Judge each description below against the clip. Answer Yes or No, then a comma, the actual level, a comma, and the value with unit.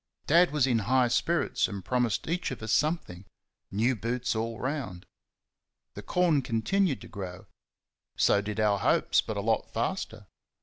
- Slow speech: No, average, 160 wpm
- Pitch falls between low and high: No, low, 120 Hz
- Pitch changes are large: Yes, wide, 5.7 semitones